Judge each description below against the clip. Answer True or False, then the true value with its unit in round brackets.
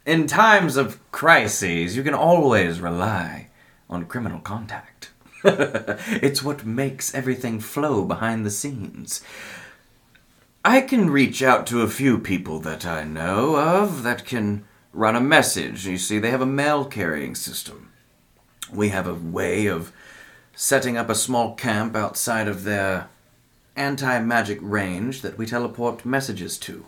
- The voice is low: True (115 Hz)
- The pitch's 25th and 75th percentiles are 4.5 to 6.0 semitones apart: True (5.1 semitones)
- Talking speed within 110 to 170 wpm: True (145 wpm)